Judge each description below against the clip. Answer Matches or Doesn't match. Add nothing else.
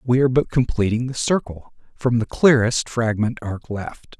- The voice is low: Matches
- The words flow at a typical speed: Matches